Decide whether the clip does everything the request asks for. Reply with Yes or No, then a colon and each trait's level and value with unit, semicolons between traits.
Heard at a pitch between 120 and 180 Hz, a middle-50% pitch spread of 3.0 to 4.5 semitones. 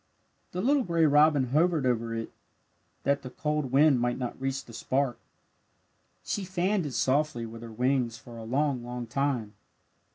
Yes: low, 135 Hz; average, 4.0 semitones